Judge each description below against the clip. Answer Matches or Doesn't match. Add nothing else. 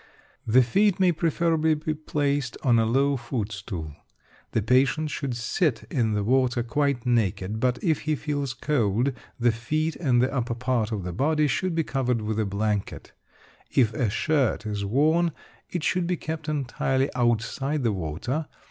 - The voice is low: Matches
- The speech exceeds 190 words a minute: Doesn't match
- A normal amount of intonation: Matches